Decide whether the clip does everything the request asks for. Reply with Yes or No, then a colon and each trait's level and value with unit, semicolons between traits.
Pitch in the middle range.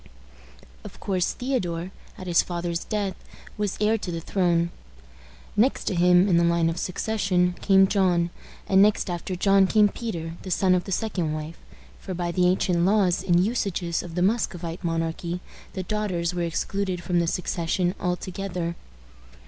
Yes: medium, 180 Hz